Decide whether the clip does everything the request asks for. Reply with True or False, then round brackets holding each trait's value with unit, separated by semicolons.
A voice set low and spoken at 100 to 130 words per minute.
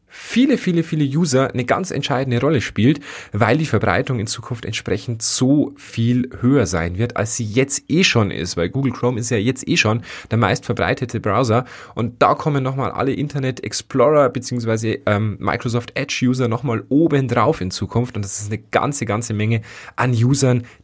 False (120 Hz; 185 wpm)